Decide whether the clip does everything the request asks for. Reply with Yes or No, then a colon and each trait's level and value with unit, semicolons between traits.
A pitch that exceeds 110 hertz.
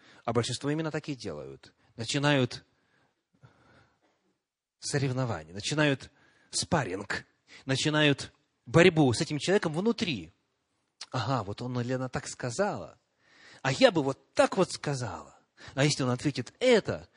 Yes: low, 135 Hz